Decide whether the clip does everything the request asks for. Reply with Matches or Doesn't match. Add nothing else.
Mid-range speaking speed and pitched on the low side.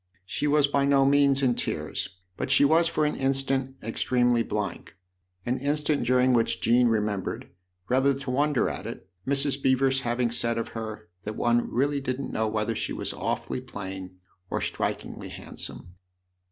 Matches